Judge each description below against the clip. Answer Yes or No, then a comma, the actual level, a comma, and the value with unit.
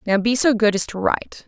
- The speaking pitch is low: No, high, 220 Hz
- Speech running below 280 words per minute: No, fast, 285 wpm